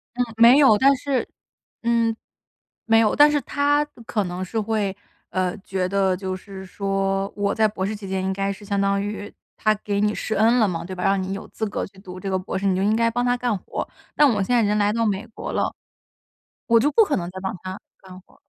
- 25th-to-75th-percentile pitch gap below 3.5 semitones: Yes, average, 3.1 semitones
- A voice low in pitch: No, high, 205 Hz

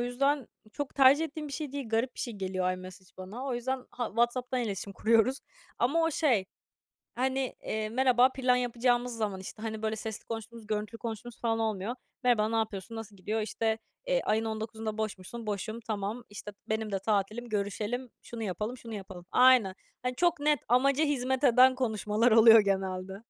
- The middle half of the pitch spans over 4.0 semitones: No, average, 3.0 semitones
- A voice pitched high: Yes, high, 225 Hz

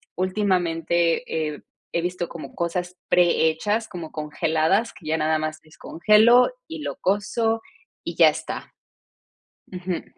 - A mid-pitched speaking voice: Yes, medium, 175 Hz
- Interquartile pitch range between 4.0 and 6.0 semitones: Yes, average, 4.3 semitones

